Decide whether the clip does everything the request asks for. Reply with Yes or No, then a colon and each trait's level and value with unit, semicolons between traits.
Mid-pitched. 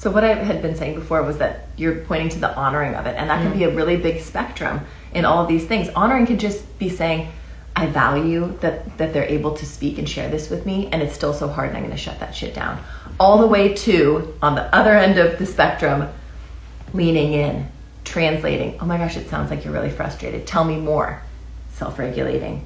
Yes: medium, 160 Hz